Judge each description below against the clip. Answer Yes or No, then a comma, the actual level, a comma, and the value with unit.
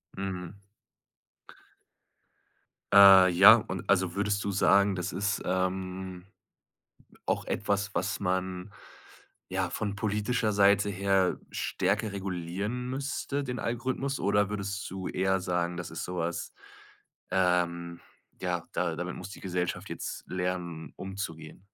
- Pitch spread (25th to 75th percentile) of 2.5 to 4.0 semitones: No, narrow, 2.0 semitones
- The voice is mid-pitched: No, very low, 95 Hz